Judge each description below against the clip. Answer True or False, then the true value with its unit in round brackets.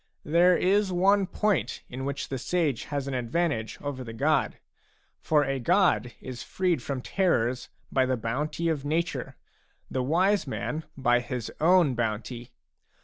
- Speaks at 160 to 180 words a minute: False (150 wpm)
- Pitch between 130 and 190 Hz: True (140 Hz)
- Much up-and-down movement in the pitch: True (5.7 semitones)